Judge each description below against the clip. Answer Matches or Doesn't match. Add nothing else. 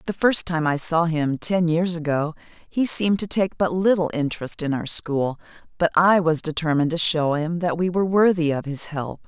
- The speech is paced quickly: Matches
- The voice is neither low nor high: Matches